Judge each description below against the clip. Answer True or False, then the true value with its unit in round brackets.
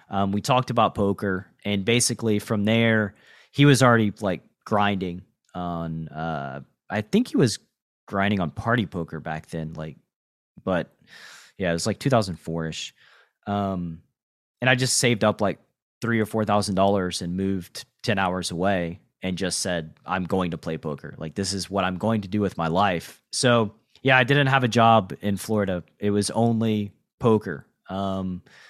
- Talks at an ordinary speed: True (170 wpm)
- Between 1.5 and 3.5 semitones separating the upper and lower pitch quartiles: False (3.9 semitones)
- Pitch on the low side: True (100 Hz)